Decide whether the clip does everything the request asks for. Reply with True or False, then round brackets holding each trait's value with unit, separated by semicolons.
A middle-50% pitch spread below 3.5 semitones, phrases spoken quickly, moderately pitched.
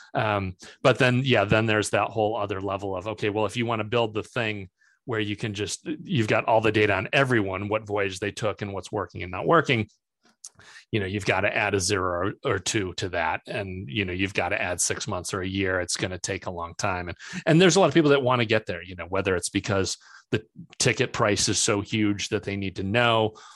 False (2.6 semitones; 255 wpm; 105 Hz)